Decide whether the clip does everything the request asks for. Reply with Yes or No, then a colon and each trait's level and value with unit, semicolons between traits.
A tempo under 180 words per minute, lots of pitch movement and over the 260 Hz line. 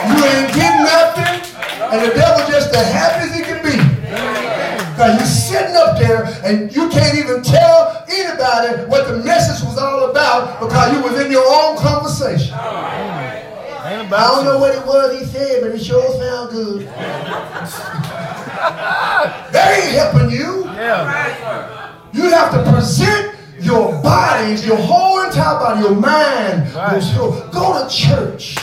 Yes: average, 150 wpm; wide, 6.6 semitones; very high, 270 Hz